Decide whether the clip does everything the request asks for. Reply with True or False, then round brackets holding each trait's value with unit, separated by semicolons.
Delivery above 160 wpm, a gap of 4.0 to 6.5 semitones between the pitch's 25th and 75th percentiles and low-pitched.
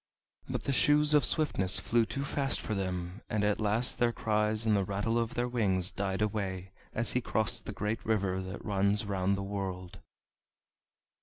False (180 wpm; 3.2 semitones; 105 Hz)